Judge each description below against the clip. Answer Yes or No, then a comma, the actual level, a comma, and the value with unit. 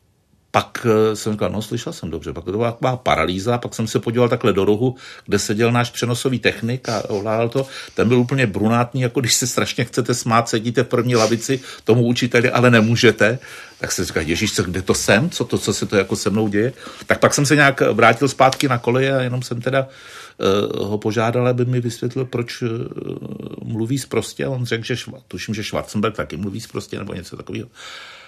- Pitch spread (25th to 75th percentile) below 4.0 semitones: Yes, narrow, 2.6 semitones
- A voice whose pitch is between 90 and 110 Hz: No, low, 120 Hz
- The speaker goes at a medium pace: No, fast, 210 wpm